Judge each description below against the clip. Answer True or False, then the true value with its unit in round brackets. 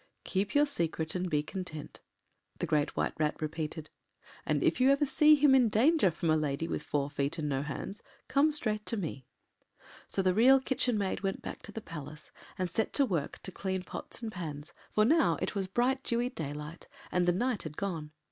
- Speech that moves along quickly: True (210 wpm)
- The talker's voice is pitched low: False (185 Hz)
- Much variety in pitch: True (7.6 semitones)